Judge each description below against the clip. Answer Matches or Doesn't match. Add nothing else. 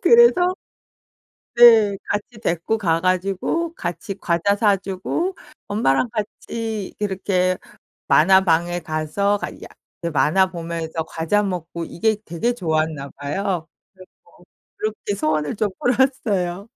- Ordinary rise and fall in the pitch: Matches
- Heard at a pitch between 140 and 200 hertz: Matches